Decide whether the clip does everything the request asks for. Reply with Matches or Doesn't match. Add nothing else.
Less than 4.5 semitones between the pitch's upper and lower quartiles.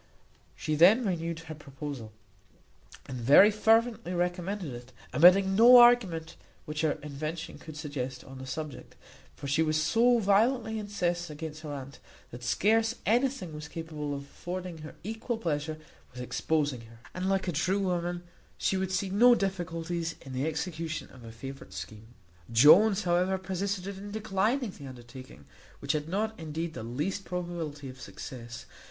Doesn't match